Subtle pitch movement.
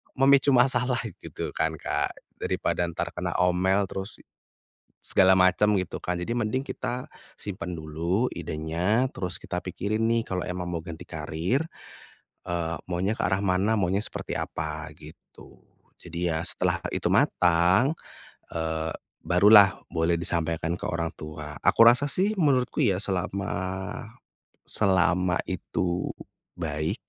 No: average, 4.1 semitones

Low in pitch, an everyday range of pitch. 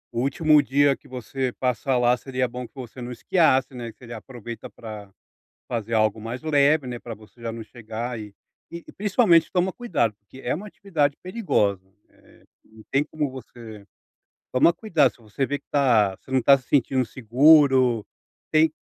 Yes: low, 125 Hz; average, 3.9 semitones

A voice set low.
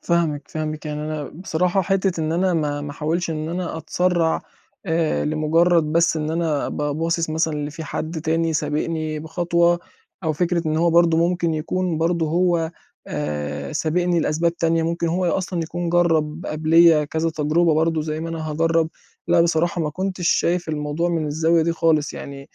No: medium, 165 Hz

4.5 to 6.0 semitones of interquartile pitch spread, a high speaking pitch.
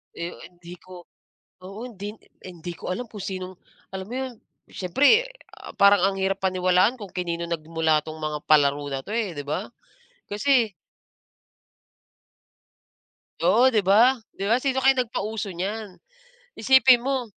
Yes: average, 5.0 semitones; high, 195 Hz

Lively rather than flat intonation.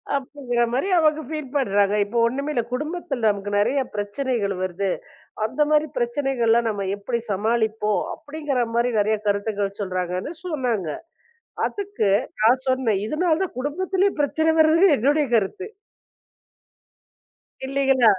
Yes: wide, 6.1 semitones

